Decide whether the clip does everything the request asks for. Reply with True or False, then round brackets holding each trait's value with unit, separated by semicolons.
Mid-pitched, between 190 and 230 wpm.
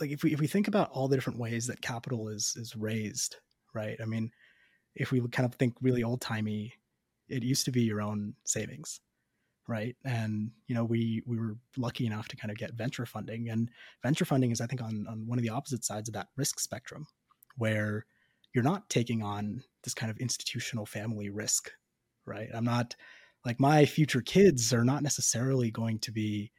False (120 Hz; 205 wpm)